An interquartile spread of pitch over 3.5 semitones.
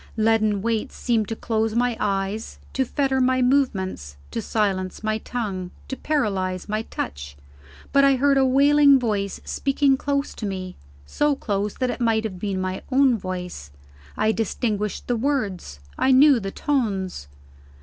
Yes: average, 5.3 semitones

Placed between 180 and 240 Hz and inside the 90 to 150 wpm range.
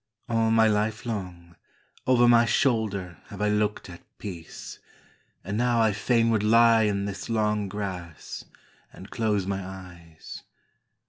No: low, 105 Hz; average, 140 wpm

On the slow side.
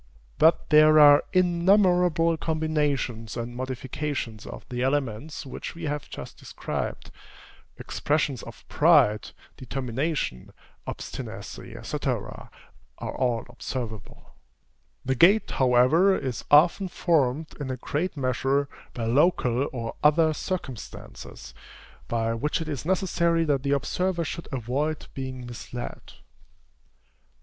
Yes: slow, 110 wpm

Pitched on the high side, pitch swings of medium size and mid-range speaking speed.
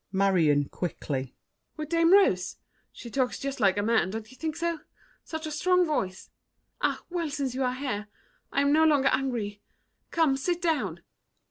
No: very high, 270 Hz; wide, 7.6 semitones; average, 170 wpm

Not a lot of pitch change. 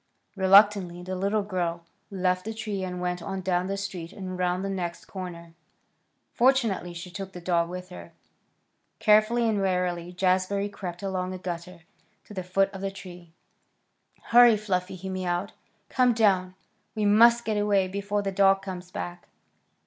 Yes: narrow, 2.0 semitones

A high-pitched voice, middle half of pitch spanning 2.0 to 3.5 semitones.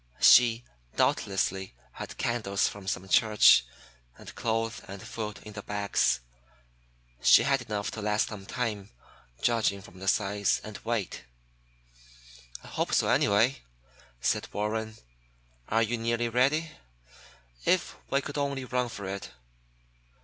No: low, 110 Hz; average, 2.8 semitones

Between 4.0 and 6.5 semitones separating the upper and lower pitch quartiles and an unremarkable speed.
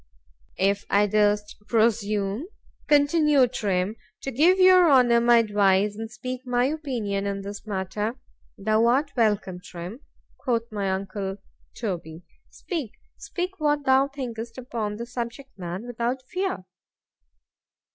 No: average, 4.6 semitones; slow, 120 wpm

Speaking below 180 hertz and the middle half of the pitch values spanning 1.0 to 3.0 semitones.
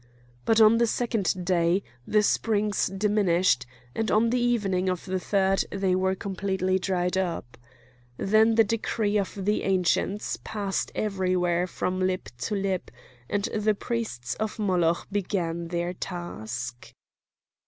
No: high, 190 Hz; average, 2.7 semitones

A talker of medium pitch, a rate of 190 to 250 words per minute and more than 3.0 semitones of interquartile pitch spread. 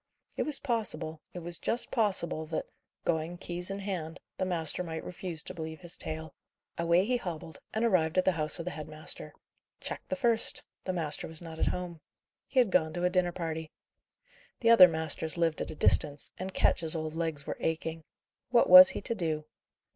No: medium, 170 Hz; average, 200 wpm; narrow, 2.6 semitones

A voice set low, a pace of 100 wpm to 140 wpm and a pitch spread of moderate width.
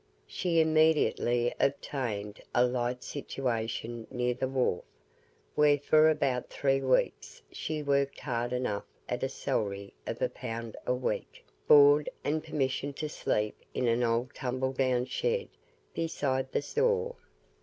Yes: low, 130 Hz; slow, 135 wpm; average, 3.4 semitones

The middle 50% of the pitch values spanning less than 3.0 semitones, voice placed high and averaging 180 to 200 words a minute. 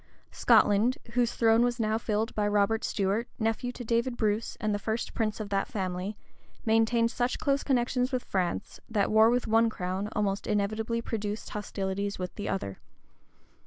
No: narrow, 2.4 semitones; high, 220 Hz; average, 165 wpm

